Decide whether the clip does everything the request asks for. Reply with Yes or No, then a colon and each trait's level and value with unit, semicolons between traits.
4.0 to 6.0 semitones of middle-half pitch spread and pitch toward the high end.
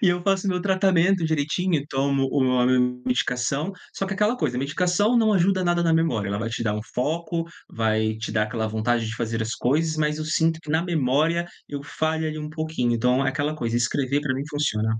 No: wide, 5.4 semitones; medium, 145 Hz